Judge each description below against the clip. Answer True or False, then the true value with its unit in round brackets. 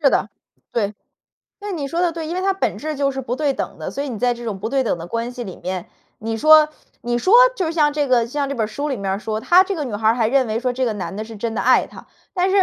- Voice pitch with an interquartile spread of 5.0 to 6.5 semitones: True (5.4 semitones)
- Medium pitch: False (255 Hz)